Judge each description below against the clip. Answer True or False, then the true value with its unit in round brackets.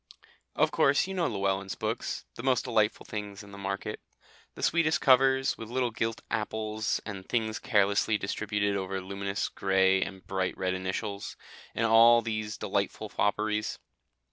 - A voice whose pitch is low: True (105 Hz)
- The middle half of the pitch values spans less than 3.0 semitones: True (2.5 semitones)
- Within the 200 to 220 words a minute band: False (150 wpm)